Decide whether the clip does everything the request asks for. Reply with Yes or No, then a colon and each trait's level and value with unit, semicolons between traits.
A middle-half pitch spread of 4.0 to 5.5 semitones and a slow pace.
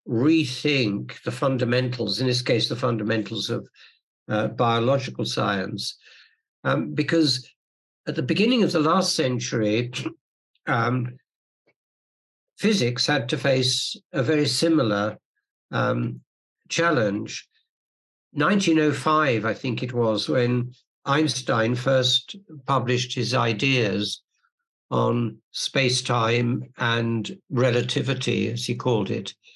Yes: average, 4.4 semitones; slow, 105 wpm